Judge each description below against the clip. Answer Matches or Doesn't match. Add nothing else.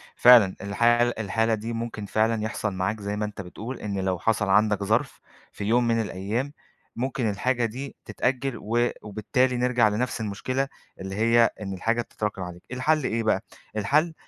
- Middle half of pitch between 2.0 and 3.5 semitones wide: Matches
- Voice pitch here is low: Matches